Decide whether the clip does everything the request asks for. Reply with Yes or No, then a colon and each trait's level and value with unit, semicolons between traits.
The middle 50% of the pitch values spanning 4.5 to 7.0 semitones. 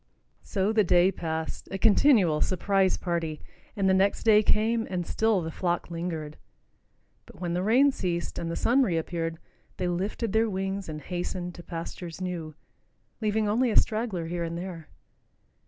No: average, 3.7 semitones